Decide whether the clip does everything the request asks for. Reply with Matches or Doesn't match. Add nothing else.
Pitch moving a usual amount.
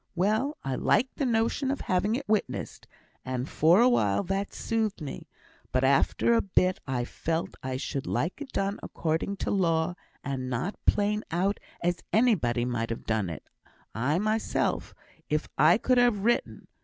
Doesn't match